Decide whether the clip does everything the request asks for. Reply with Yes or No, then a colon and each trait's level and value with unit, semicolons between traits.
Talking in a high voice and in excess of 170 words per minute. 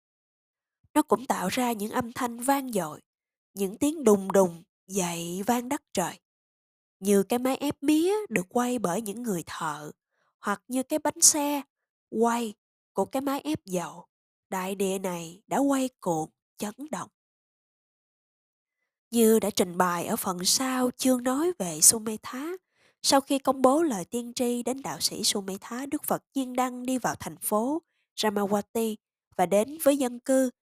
No: high, 235 Hz; slow, 165 wpm